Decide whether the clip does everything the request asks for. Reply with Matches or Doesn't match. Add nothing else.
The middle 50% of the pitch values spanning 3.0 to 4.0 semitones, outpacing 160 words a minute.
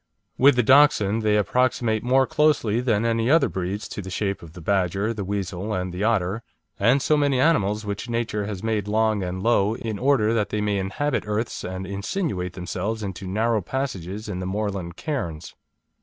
Matches